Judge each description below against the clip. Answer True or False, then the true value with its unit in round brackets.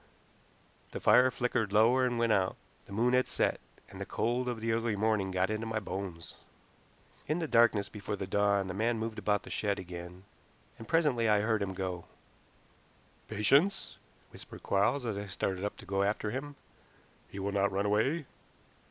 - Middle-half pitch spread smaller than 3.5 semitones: True (3.1 semitones)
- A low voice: True (105 Hz)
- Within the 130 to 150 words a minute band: False (180 wpm)